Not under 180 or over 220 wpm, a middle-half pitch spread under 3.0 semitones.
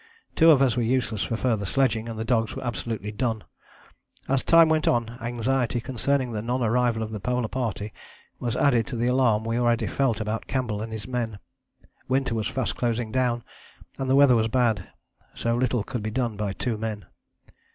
Yes: average, 195 wpm; narrow, 2.5 semitones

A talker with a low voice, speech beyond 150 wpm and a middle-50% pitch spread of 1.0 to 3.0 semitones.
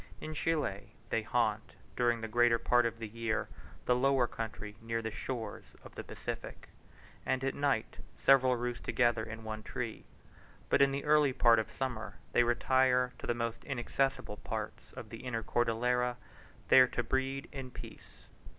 Yes: low, 120 Hz; average, 170 wpm; narrow, 2.4 semitones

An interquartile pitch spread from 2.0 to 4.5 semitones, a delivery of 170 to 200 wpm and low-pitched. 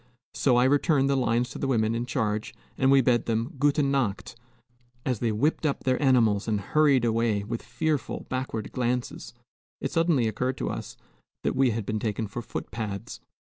Yes: average, 3.4 semitones; average, 180 wpm; low, 120 Hz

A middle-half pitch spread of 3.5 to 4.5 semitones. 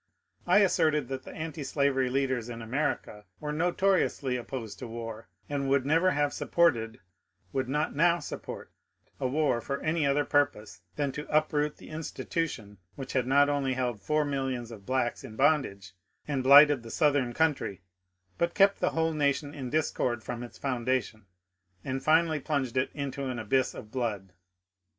Yes: average, 3.8 semitones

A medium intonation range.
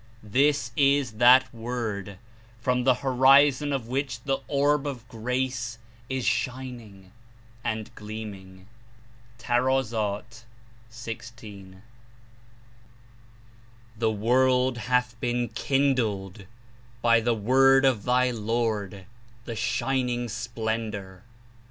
Yes: average, 3.1 semitones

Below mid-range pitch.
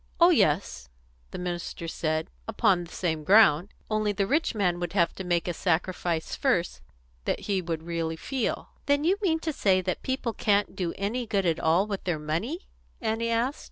No: high, 190 Hz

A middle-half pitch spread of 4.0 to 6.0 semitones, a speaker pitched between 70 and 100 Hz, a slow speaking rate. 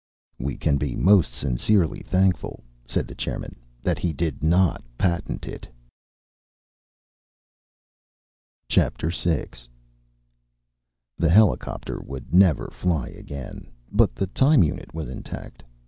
Yes: average, 4.8 semitones; very low, 80 Hz; slow, 105 wpm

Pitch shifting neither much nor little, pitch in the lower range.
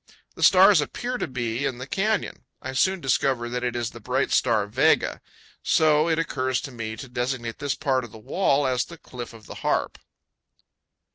Yes: average, 3.3 semitones; low, 130 Hz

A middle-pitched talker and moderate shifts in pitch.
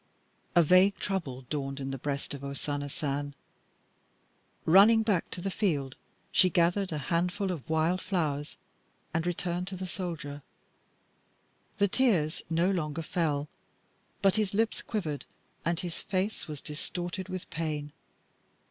Yes: medium, 170 Hz; average, 4.2 semitones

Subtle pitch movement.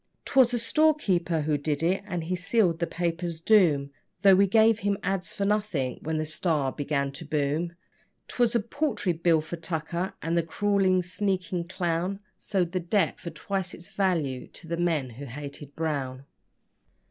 No: average, 3.9 semitones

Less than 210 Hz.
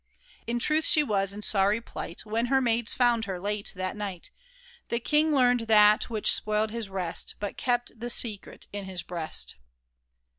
No: high, 215 Hz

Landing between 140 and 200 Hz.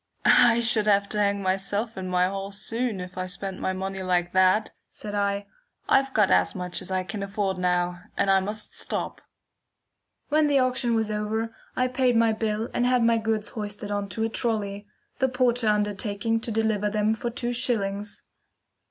No: high, 210 Hz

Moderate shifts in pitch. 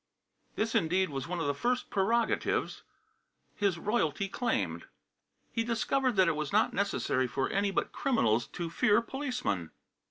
No: wide, 7.1 semitones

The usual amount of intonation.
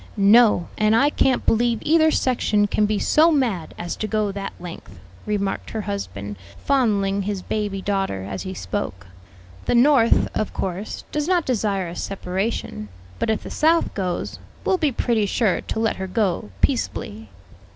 Yes: average, 3.9 semitones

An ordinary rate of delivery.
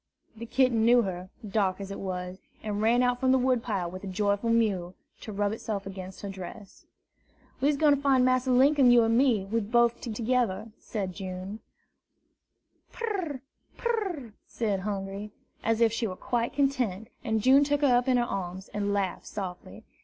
Yes: average, 185 wpm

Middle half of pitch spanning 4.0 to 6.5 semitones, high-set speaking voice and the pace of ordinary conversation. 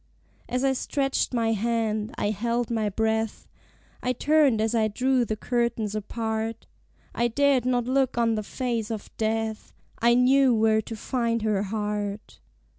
No: narrow, 2.4 semitones; high, 230 Hz; average, 155 wpm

